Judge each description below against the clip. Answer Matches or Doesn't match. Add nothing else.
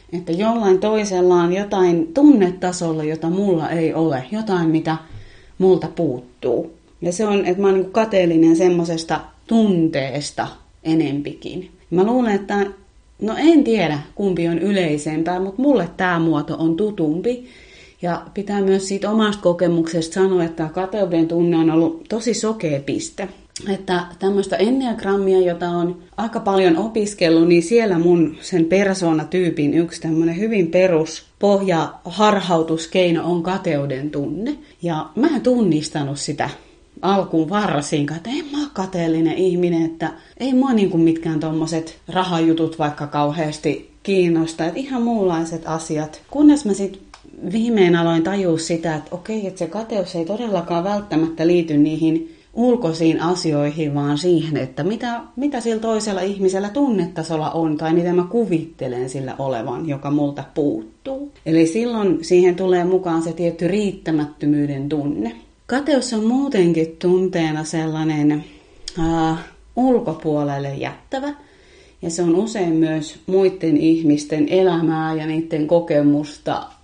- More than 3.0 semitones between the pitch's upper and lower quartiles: Matches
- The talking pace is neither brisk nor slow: Matches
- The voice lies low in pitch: Doesn't match